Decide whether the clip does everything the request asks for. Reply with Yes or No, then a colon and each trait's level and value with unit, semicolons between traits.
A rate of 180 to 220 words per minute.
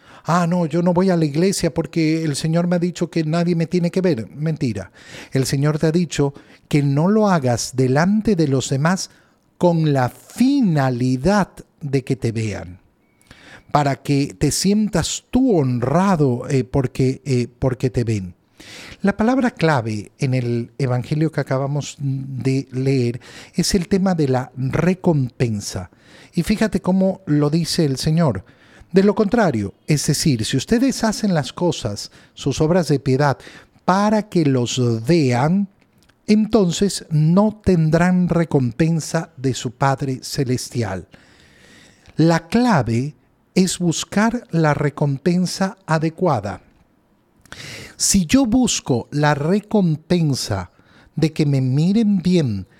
No: average, 135 wpm